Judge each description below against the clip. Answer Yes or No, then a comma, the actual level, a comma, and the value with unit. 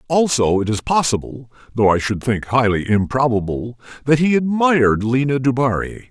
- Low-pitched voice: Yes, low, 125 Hz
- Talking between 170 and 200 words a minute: No, average, 145 wpm